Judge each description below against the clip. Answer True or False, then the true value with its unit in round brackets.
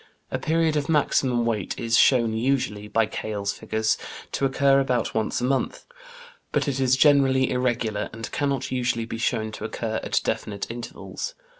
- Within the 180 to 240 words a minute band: False (165 wpm)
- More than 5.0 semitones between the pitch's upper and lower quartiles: False (3.5 semitones)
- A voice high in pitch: False (120 Hz)